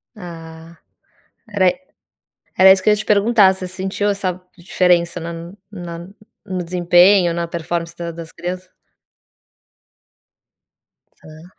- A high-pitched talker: No, medium, 180 Hz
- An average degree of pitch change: No, narrow, 2.1 semitones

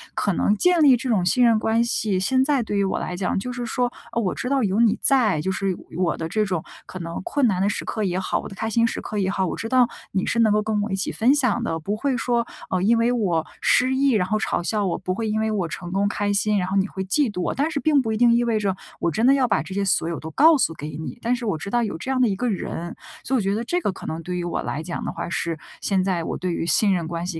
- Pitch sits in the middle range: No, high, 210 Hz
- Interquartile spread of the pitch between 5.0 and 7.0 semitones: No, average, 4.5 semitones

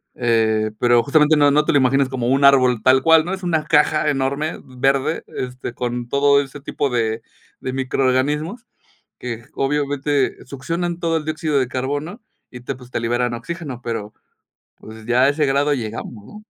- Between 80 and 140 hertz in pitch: Yes, low, 135 Hz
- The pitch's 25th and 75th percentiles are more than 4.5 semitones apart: No, average, 3.3 semitones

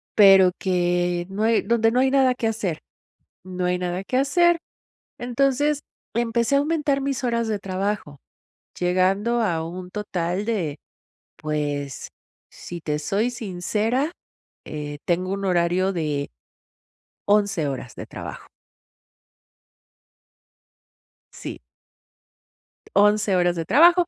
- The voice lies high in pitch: Yes, high, 195 Hz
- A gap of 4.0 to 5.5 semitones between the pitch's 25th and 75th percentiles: Yes, average, 5.1 semitones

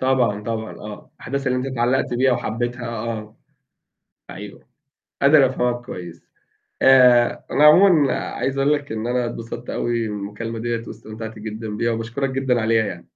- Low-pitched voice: Yes, low, 120 Hz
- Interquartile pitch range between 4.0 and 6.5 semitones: No, average, 2.9 semitones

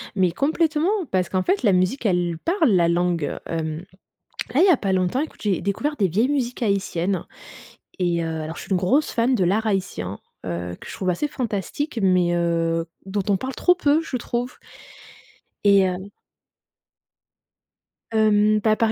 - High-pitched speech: Yes, high, 195 Hz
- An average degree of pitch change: No, wide, 5.9 semitones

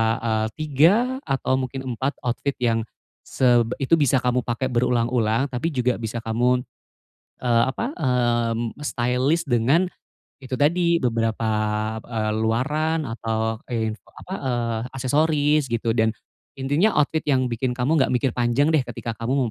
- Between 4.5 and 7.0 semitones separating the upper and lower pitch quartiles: No, average, 3.6 semitones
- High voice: No, low, 125 Hz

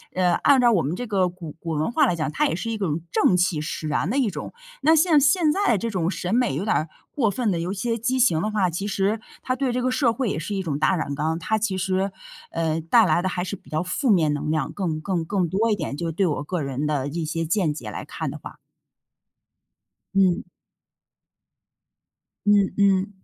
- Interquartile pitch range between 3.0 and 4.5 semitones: No, average, 5.2 semitones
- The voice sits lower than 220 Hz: Yes, medium, 185 Hz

